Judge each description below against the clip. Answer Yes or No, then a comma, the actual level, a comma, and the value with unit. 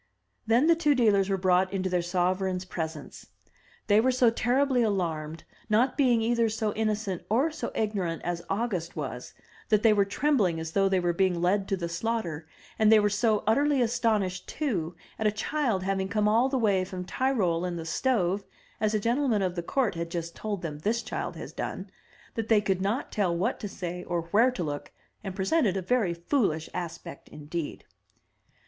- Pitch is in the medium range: No, high, 200 Hz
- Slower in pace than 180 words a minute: No, average, 190 wpm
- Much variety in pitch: No, average, 4.5 semitones